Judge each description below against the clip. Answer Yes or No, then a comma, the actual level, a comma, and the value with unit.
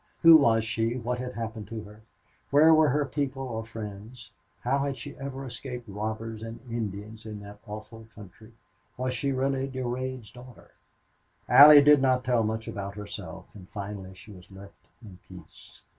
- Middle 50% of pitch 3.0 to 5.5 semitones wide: Yes, average, 3.6 semitones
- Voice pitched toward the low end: Yes, low, 115 Hz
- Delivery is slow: No, average, 170 wpm